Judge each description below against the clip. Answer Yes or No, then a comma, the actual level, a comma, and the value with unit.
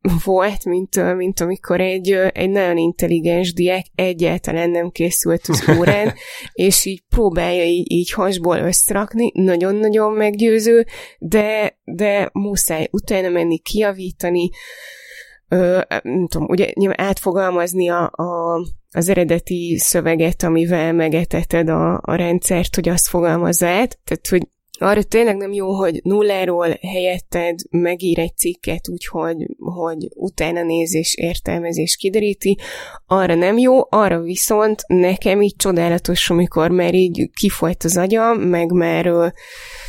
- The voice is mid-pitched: Yes, medium, 180 Hz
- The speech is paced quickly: No, average, 120 wpm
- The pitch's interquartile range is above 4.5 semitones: No, narrow, 2.4 semitones